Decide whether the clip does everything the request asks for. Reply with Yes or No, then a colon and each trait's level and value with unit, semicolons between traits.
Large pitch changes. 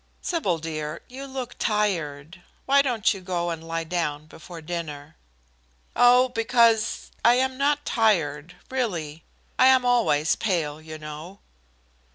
Yes: wide, 7.6 semitones